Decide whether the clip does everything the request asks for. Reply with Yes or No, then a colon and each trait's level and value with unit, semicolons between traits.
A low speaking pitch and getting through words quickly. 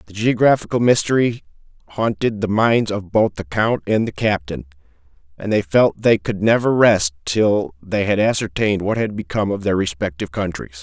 No: low, 100 Hz; average, 170 wpm